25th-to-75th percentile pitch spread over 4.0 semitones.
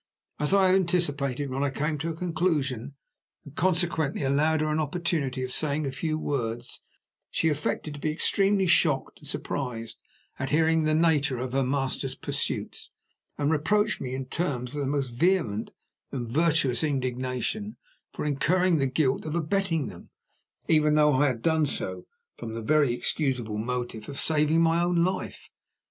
No: average, 3.7 semitones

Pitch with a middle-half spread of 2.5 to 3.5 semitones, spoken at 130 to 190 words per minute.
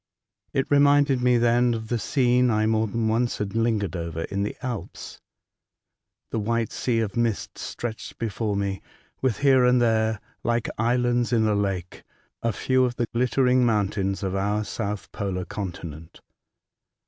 Yes: average, 3.2 semitones; average, 160 wpm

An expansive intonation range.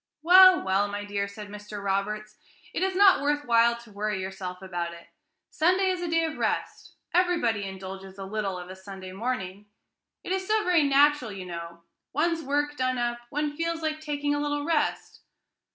Yes: wide, 8.0 semitones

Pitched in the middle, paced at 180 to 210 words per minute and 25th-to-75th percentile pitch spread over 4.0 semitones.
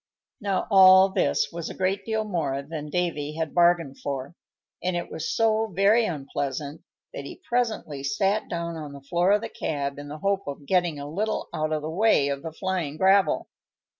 Yes: medium, 170 Hz; average, 195 wpm; average, 4.9 semitones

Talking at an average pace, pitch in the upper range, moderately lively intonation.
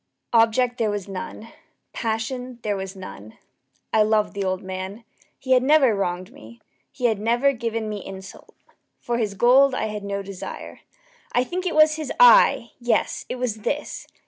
Yes: average, 170 wpm; high, 225 Hz; average, 4.1 semitones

